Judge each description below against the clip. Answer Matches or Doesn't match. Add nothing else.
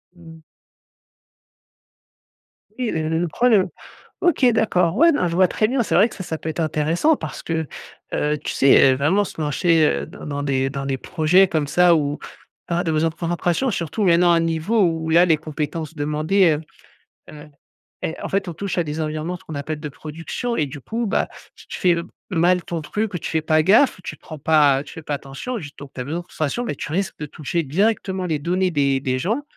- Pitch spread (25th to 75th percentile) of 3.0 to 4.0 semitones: Matches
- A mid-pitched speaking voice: Matches